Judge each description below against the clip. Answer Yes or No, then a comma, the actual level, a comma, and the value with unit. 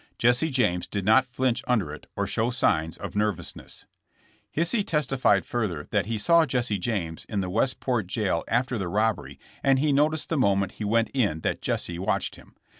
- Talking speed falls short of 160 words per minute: No, average, 190 wpm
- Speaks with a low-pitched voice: Yes, low, 110 Hz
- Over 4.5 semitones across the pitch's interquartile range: Yes, average, 5.1 semitones